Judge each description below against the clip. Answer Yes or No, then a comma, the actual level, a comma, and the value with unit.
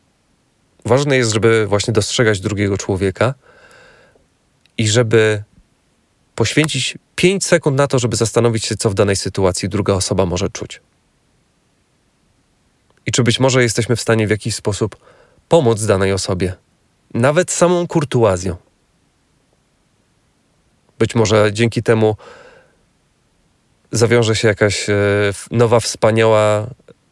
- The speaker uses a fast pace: No, average, 115 wpm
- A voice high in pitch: No, low, 110 Hz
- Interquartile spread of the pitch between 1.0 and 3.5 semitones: Yes, average, 3.0 semitones